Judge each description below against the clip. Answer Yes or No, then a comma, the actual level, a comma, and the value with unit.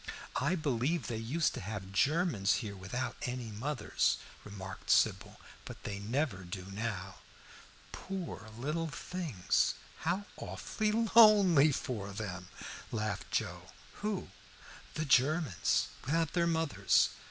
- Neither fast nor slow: No, slow, 120 wpm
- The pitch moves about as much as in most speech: No, wide, 8.3 semitones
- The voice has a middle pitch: No, low, 130 Hz